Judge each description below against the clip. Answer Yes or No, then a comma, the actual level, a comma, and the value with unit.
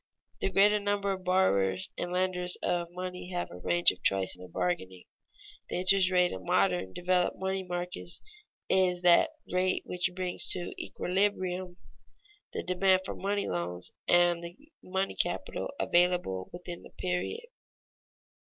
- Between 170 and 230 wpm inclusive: No, average, 145 wpm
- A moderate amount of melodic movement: No, narrow, 1.5 semitones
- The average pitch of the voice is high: No, medium, 180 Hz